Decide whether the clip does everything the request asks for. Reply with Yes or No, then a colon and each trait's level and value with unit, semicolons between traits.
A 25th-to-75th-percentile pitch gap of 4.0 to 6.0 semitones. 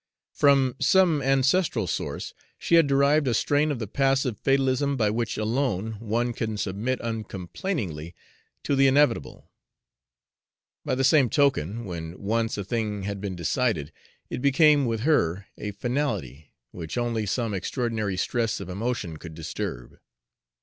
Yes: wide, 5.4 semitones